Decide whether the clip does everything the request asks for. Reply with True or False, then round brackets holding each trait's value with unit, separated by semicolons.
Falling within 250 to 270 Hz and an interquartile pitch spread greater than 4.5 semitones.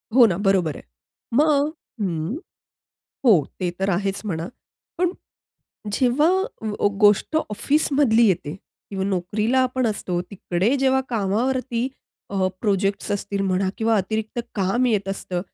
False (210 Hz; 4.9 semitones)